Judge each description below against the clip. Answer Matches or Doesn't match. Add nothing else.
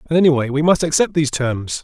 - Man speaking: Matches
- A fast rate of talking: Matches